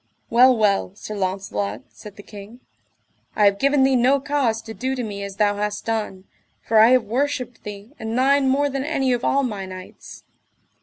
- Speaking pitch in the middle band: No, high, 225 Hz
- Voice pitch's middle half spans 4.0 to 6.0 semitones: Yes, average, 4.4 semitones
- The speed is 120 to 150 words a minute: No, average, 195 wpm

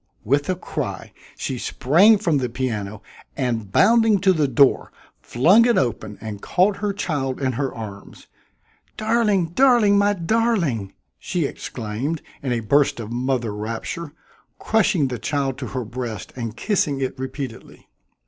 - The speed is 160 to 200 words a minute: No, average, 150 wpm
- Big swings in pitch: Yes, wide, 8.4 semitones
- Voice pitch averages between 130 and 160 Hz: Yes, low, 135 Hz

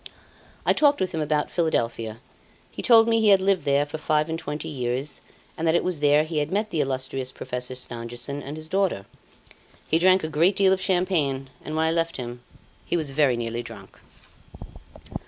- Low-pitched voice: No, medium, 155 Hz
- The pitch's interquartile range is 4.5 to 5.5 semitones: Yes, average, 5.0 semitones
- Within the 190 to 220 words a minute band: Yes, average, 195 wpm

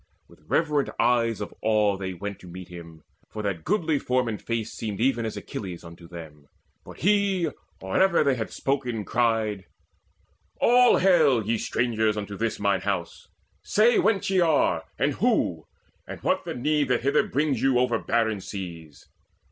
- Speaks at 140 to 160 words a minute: No, average, 170 wpm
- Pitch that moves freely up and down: Yes, wide, 6.2 semitones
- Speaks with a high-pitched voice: No, low, 115 Hz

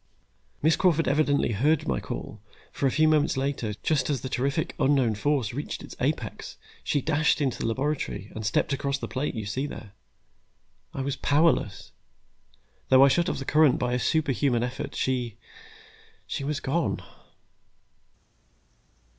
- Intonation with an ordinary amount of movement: Yes, average, 3.4 semitones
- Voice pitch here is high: No, medium, 140 Hz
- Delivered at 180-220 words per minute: No, average, 155 wpm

